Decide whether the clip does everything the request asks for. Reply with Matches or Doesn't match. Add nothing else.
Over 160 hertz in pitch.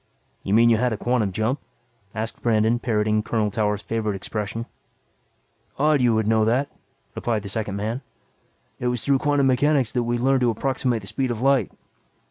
Doesn't match